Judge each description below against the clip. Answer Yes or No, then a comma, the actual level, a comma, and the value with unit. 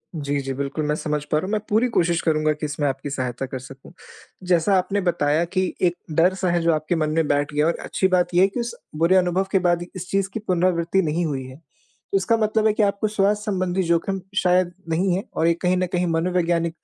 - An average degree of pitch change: Yes, average, 3.5 semitones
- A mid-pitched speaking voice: Yes, medium, 175 Hz